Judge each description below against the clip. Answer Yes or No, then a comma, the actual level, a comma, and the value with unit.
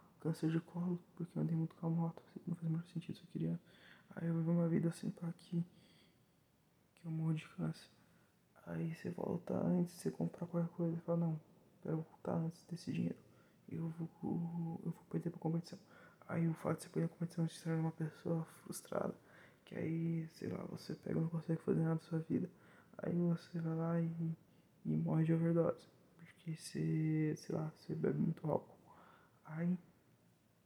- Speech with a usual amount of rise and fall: No, narrow, 1.2 semitones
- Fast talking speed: Yes, fast, 195 wpm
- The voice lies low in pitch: No, medium, 165 Hz